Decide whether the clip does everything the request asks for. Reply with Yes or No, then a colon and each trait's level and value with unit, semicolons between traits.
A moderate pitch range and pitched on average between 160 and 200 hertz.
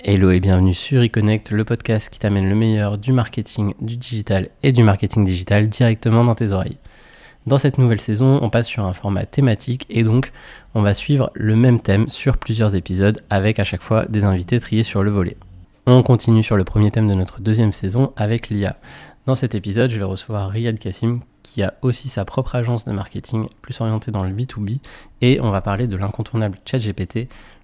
No: average, 3.1 semitones; low, 110 Hz